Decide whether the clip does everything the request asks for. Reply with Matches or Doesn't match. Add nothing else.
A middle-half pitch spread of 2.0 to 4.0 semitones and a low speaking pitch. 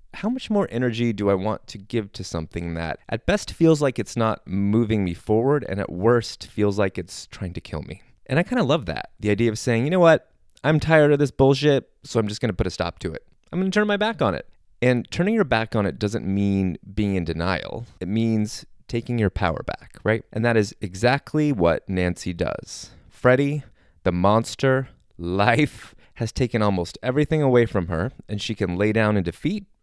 Doesn't match